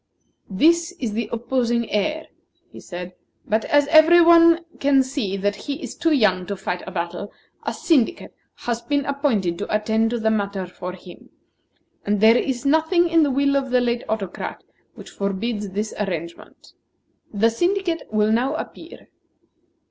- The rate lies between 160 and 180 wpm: Yes, average, 165 wpm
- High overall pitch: Yes, high, 235 Hz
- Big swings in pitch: Yes, wide, 6.1 semitones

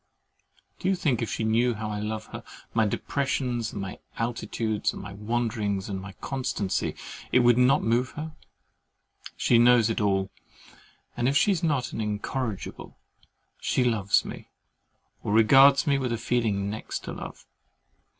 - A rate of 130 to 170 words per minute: Yes, average, 160 wpm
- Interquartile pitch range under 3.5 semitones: Yes, average, 3.1 semitones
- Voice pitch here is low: Yes, low, 115 Hz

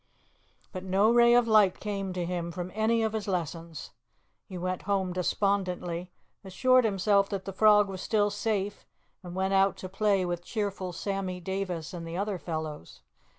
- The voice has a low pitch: No, high, 195 Hz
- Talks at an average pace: Yes, average, 170 wpm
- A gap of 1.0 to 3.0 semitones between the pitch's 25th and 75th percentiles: Yes, narrow, 2.4 semitones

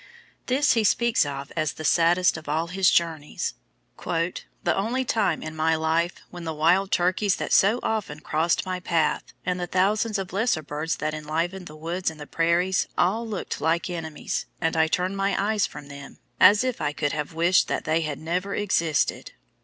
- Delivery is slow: No, average, 190 wpm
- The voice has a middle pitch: Yes, medium, 170 Hz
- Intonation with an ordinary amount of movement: Yes, average, 3.5 semitones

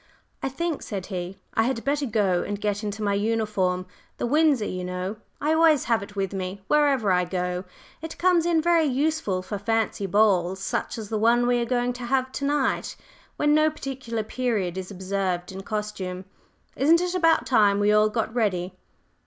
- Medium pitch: No, high, 220 Hz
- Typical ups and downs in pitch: No, wide, 5.8 semitones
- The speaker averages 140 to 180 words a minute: No, average, 190 wpm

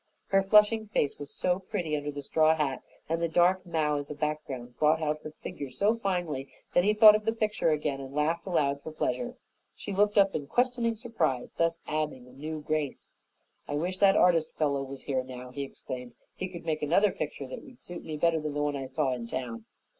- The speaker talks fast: Yes, fast, 220 wpm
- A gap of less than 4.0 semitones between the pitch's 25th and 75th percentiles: No, average, 4.9 semitones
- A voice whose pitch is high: No, medium, 155 Hz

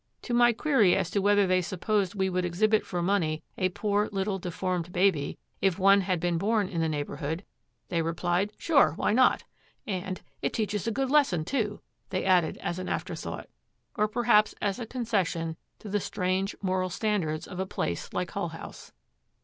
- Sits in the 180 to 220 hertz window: Yes, high, 190 Hz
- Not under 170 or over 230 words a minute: Yes, average, 180 wpm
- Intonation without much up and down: No, average, 3.0 semitones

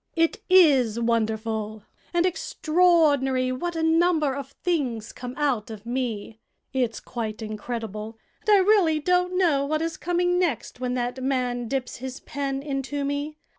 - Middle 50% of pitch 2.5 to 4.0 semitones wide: No, wide, 5.5 semitones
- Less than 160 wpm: Yes, average, 150 wpm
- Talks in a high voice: Yes, very high, 270 Hz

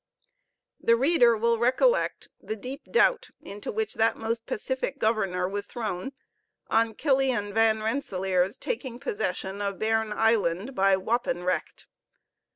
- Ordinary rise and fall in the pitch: Yes, average, 3.4 semitones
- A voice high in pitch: Yes, high, 220 Hz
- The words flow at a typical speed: No, slow, 130 wpm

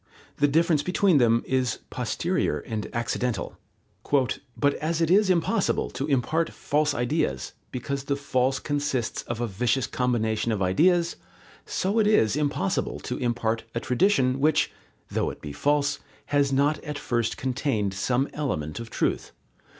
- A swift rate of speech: No, average, 150 wpm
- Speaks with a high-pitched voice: No, low, 135 Hz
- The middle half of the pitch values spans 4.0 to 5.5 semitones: Yes, average, 4.3 semitones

